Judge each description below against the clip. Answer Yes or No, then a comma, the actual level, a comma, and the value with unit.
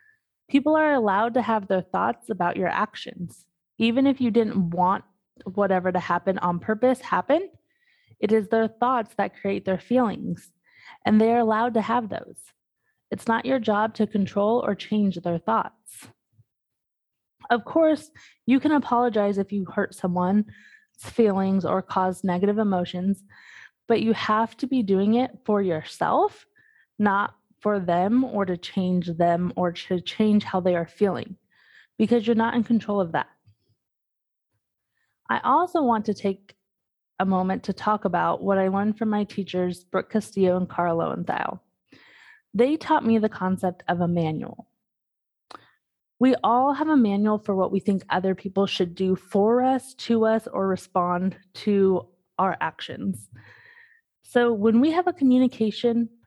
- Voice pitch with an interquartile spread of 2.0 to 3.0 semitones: No, average, 4.2 semitones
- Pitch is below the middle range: No, high, 210 Hz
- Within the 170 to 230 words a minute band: No, average, 155 wpm